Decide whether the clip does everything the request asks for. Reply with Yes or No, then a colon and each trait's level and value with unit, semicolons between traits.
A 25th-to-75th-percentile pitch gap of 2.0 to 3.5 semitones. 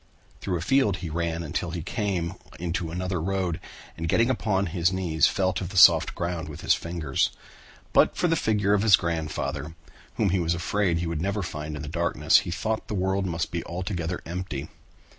Yes: average, 2.7 semitones